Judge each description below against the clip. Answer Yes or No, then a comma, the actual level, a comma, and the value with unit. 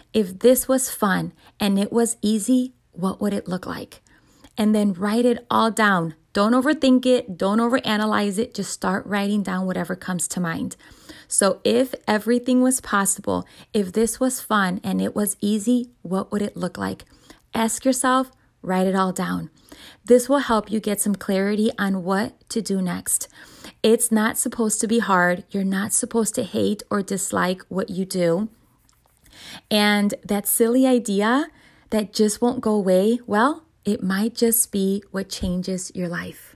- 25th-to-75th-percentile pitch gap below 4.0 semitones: Yes, average, 3.6 semitones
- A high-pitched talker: Yes, high, 210 Hz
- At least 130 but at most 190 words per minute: Yes, average, 170 wpm